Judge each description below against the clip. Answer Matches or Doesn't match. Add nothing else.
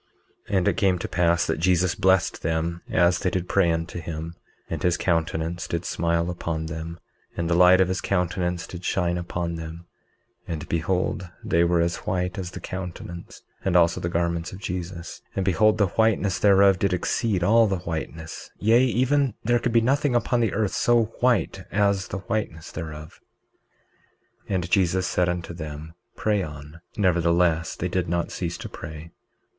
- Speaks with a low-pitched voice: Matches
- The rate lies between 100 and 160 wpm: Doesn't match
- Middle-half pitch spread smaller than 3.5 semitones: Matches